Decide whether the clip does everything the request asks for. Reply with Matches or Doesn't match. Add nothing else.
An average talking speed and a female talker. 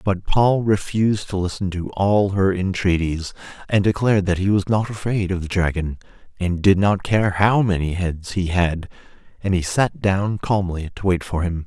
Doesn't match